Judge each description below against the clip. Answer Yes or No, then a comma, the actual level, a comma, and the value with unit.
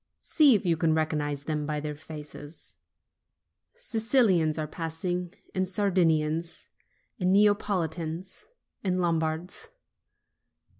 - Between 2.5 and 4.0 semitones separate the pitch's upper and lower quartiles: Yes, average, 3.2 semitones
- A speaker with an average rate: No, slow, 100 wpm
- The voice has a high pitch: No, medium, 165 Hz